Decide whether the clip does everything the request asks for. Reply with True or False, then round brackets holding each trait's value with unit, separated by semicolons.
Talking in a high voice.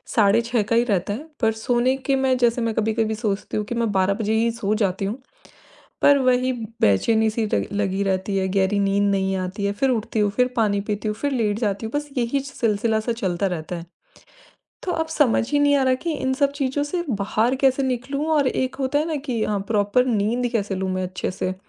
True (225 Hz)